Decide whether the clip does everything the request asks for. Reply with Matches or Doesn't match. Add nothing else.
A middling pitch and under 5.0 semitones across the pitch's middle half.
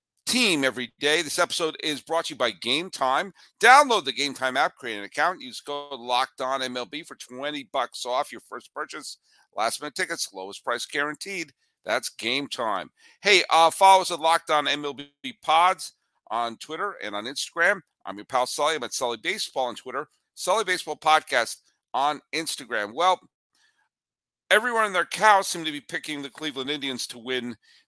Doesn't match